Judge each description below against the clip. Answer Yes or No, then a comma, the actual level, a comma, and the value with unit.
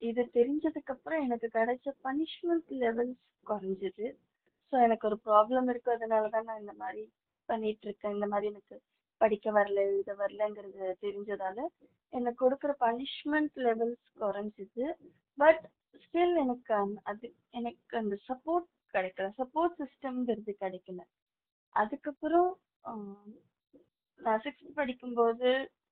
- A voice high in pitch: Yes, high, 235 Hz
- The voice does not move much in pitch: No, average, 4.9 semitones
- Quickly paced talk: No, average, 105 wpm